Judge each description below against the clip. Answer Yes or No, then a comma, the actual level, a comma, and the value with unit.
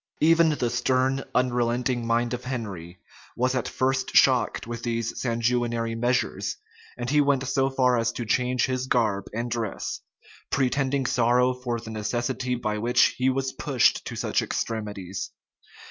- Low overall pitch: Yes, low, 125 Hz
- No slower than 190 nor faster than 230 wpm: No, average, 150 wpm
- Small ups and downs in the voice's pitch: Yes, narrow, 1.9 semitones